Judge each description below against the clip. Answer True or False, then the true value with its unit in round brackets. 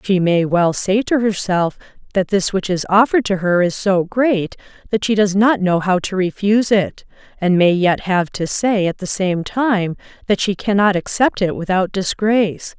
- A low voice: False (195 Hz)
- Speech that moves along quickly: False (195 wpm)